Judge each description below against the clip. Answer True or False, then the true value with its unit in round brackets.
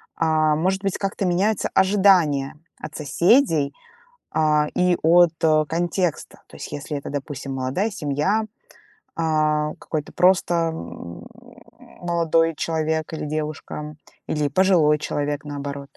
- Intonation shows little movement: False (3.1 semitones)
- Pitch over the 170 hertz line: False (155 Hz)